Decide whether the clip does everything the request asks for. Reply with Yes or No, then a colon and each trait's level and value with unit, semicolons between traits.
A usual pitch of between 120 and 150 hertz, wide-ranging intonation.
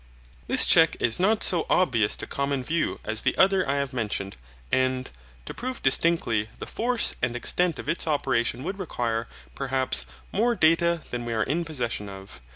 Yes: low, 135 Hz; wide, 6.3 semitones